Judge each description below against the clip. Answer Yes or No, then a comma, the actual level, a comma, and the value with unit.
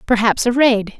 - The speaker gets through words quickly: No, average, 180 wpm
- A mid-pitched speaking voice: No, high, 230 Hz